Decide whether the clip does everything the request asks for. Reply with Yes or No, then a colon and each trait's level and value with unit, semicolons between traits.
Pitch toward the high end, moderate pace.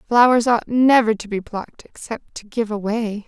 Yes: high, 225 Hz; average, 185 wpm